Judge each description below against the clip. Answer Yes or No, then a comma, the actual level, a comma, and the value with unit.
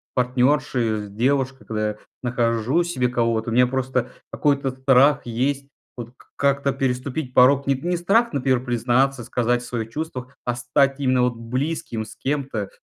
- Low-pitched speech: Yes, low, 125 Hz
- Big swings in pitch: No, narrow, 2.5 semitones